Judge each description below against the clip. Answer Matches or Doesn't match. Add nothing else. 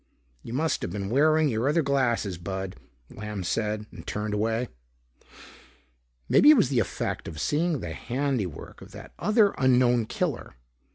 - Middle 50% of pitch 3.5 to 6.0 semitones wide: Matches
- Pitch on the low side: Matches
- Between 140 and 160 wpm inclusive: Matches